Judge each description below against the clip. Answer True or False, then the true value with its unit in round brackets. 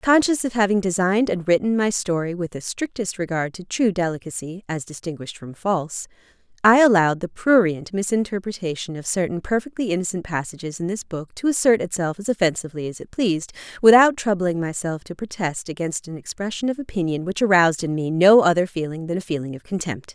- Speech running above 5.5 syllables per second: True (5.9 syllables/s)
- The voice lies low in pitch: False (185 Hz)